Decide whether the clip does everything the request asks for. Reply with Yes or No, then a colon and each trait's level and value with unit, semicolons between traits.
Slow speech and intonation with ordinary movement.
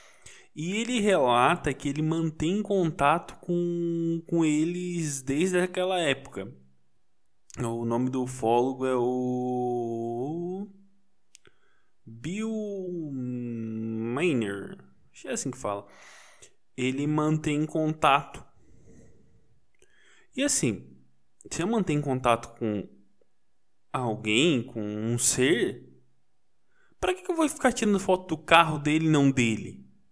No: slow, 105 wpm; wide, 7.0 semitones